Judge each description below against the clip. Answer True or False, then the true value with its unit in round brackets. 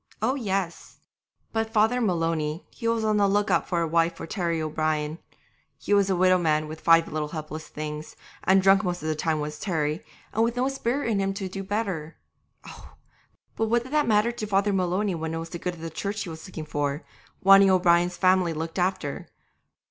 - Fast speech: True (210 wpm)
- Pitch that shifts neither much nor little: True (4.3 semitones)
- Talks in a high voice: False (180 Hz)